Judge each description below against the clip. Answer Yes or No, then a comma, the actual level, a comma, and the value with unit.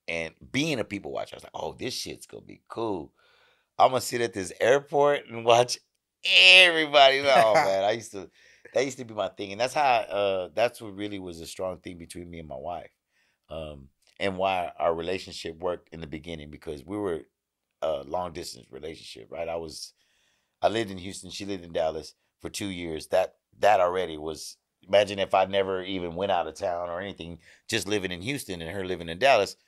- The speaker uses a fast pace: Yes, fast, 210 wpm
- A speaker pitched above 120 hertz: No, very low, 95 Hz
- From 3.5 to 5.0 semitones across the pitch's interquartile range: Yes, average, 4.2 semitones